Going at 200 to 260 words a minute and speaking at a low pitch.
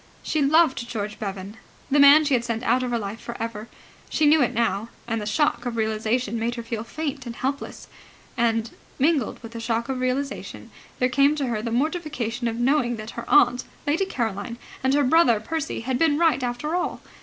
No: fast, 205 wpm; high, 245 Hz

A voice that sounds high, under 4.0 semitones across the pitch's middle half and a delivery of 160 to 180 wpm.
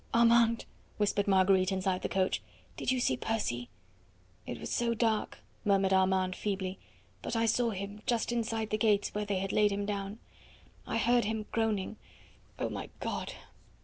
Yes: high, 205 Hz; average, 2.8 semitones; average, 165 wpm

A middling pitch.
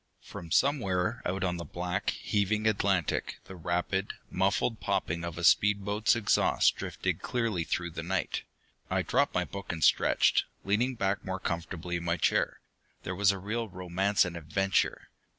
No: very low, 95 Hz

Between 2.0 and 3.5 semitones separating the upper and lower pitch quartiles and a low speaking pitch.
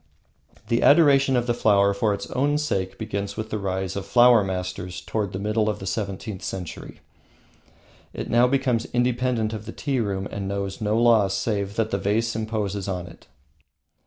Yes: average, 3.2 semitones; low, 105 Hz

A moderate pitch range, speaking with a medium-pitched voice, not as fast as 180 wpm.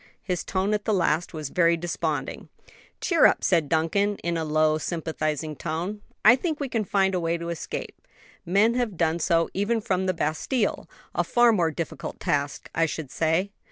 No: average, 4.2 semitones; medium, 170 Hz; average, 185 wpm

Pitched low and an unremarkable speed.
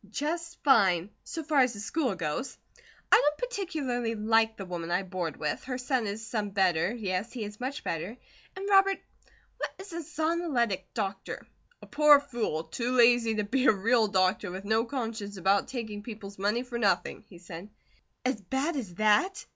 No: high, 225 Hz; average, 180 wpm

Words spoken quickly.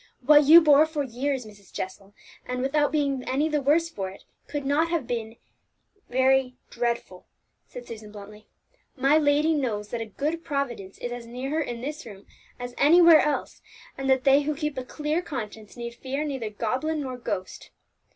No: average, 180 wpm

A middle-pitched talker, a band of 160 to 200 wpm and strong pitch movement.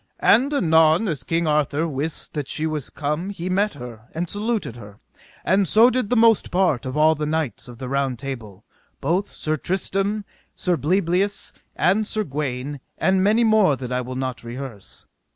Yes: medium, 160 Hz; average, 180 wpm; wide, 6.6 semitones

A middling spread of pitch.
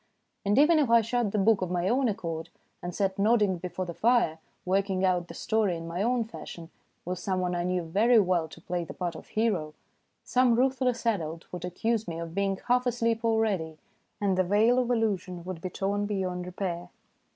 Yes: average, 4.3 semitones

